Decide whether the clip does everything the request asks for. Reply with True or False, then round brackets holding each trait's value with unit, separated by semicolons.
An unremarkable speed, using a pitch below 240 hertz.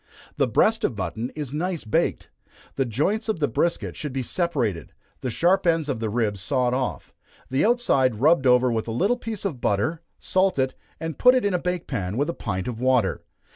False (210 wpm; 135 Hz)